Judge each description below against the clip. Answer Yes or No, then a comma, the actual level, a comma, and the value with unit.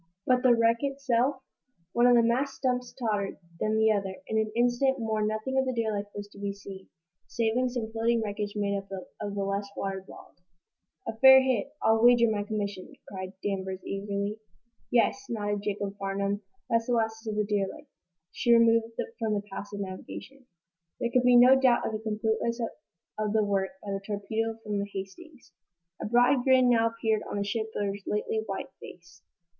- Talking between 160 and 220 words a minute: Yes, average, 185 wpm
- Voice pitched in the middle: No, high, 220 Hz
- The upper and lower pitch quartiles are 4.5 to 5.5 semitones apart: No, average, 3.0 semitones